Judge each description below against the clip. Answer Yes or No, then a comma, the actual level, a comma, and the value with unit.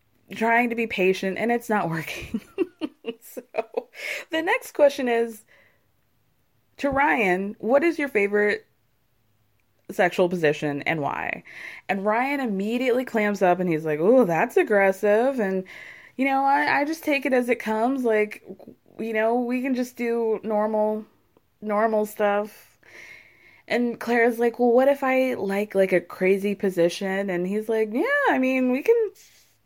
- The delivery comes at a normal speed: Yes, average, 150 wpm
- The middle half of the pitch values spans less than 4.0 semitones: No, average, 4.6 semitones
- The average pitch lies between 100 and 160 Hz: No, high, 225 Hz